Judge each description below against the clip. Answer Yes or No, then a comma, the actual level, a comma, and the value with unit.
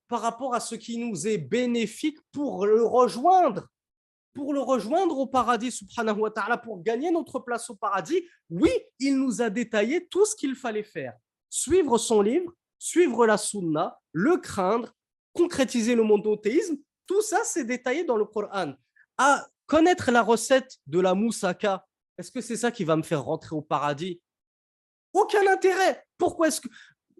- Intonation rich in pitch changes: Yes, wide, 6.7 semitones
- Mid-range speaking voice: No, high, 240 Hz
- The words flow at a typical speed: Yes, average, 170 wpm